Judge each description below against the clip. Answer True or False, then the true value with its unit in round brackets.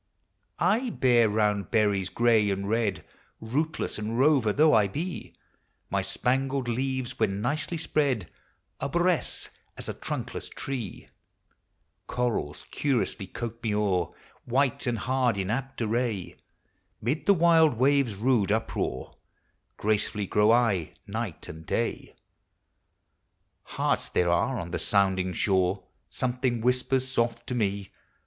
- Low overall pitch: True (115 Hz)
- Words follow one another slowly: True (125 wpm)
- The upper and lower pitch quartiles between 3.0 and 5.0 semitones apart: True (4.5 semitones)